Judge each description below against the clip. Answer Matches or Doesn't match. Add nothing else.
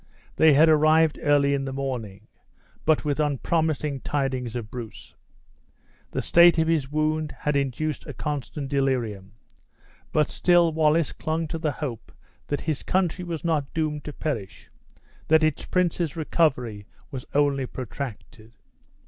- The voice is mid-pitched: Matches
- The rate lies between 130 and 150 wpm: Matches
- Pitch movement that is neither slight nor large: Matches